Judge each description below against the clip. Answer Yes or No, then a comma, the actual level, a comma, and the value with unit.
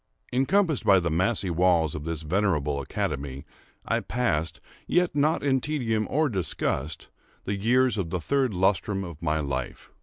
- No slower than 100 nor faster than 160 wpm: Yes, average, 155 wpm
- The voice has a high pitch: No, very low, 95 Hz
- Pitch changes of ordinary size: No, wide, 8.0 semitones